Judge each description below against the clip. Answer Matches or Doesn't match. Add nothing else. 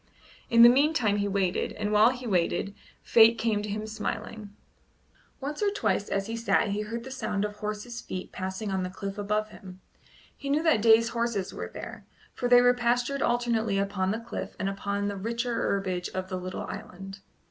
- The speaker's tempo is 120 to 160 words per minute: Doesn't match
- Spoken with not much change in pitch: Doesn't match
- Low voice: Doesn't match